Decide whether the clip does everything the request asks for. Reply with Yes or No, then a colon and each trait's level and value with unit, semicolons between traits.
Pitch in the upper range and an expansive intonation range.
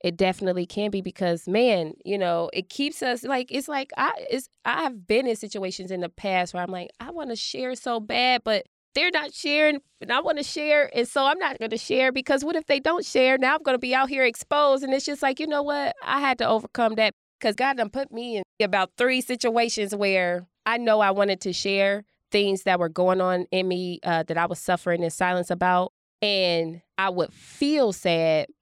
Yes: high, 220 Hz; wide, 6.5 semitones